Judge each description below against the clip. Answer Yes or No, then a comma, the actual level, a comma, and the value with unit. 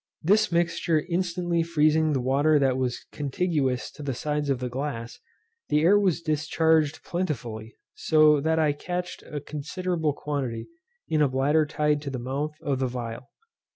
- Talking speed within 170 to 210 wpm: No, average, 160 wpm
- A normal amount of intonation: Yes, average, 3.3 semitones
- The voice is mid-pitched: Yes, medium, 150 Hz